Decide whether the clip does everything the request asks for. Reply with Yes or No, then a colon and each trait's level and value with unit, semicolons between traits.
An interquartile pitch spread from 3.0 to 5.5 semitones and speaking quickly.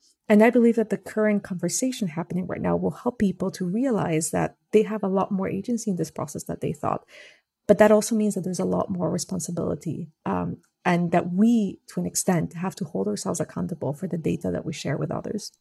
Yes: average, 3.6 semitones; fast, 225 wpm